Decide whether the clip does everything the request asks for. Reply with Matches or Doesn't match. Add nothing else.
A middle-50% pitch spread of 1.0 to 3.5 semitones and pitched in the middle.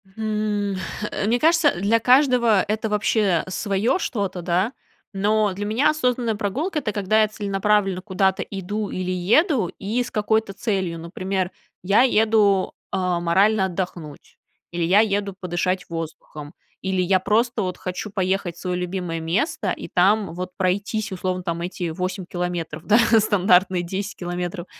Doesn't match